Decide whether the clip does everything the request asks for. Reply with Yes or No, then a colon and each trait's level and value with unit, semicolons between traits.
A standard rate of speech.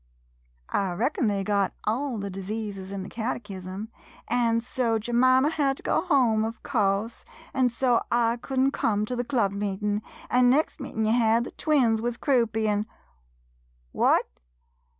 Yes: average, 165 wpm